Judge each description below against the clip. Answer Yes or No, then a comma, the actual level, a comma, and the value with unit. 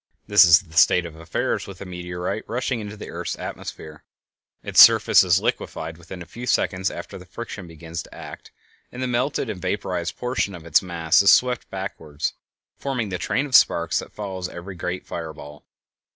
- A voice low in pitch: Yes, very low, 90 Hz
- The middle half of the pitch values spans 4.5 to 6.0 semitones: No, average, 3.7 semitones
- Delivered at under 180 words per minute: No, average, 190 wpm